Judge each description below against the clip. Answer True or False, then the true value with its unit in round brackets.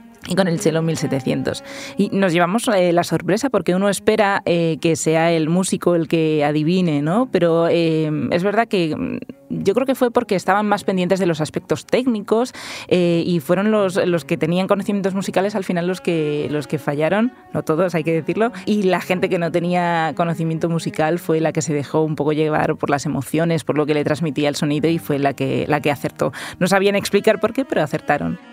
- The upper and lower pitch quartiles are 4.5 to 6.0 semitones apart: False (4.1 semitones)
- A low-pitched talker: False (175 Hz)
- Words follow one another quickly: True (210 wpm)